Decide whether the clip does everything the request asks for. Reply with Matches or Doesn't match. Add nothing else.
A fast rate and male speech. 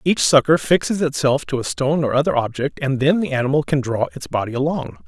Matches